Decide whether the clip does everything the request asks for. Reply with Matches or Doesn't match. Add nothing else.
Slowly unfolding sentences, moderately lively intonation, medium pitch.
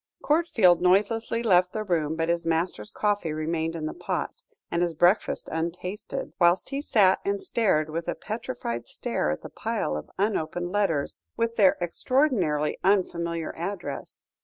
Doesn't match